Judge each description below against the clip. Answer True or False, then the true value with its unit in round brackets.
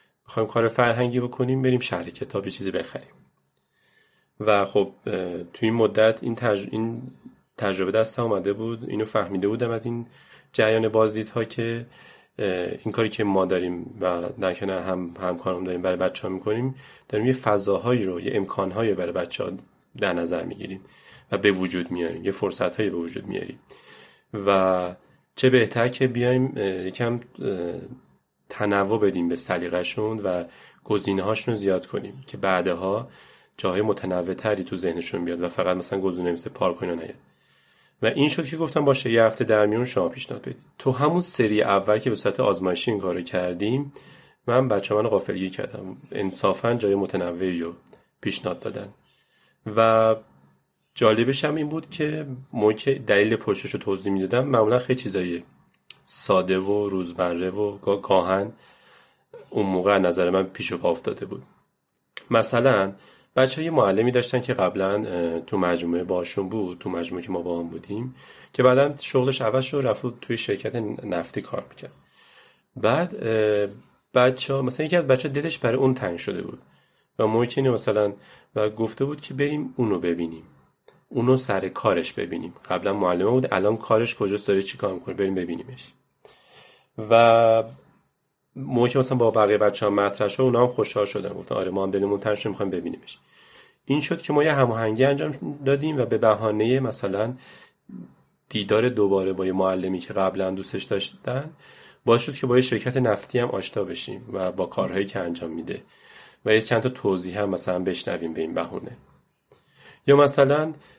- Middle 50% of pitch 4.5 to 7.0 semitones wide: True (5.0 semitones)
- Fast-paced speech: True (160 wpm)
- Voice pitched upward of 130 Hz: False (110 Hz)